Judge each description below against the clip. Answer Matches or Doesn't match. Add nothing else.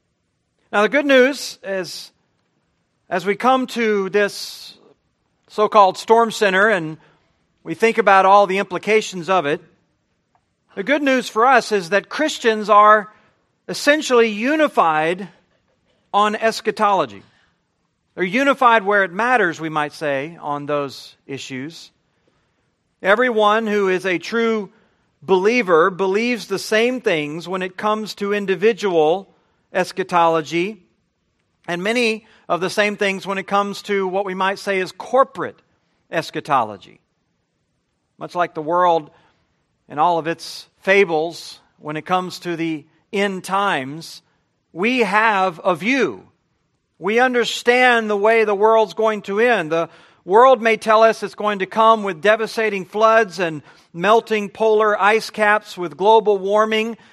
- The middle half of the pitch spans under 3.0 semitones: Doesn't match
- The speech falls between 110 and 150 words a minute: Matches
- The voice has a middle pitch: Doesn't match